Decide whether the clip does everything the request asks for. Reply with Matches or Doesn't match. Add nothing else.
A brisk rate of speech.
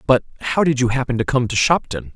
Matches